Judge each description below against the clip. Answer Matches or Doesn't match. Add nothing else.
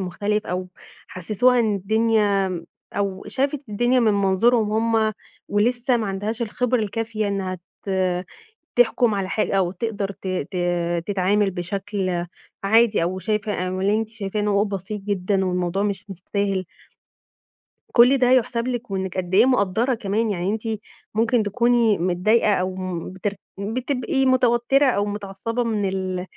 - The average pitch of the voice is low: Doesn't match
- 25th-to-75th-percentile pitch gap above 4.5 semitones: Doesn't match